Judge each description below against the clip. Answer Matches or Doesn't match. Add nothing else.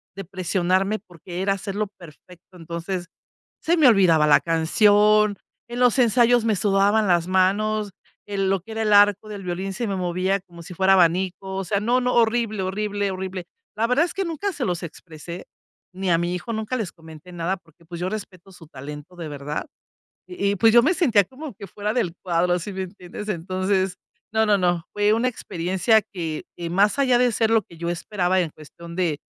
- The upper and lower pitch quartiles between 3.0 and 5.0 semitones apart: Matches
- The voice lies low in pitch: Doesn't match